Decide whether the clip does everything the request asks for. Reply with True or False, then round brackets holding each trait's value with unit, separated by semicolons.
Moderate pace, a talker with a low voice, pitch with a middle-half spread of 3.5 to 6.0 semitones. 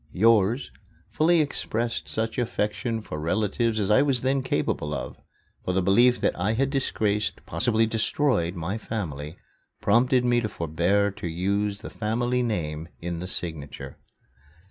True (145 wpm; 105 Hz; 5.2 semitones)